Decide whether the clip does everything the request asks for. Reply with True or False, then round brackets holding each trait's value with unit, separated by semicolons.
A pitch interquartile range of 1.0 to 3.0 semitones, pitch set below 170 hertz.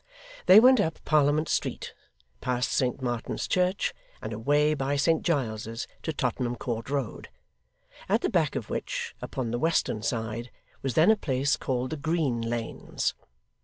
False (4.7 semitones; 135 Hz)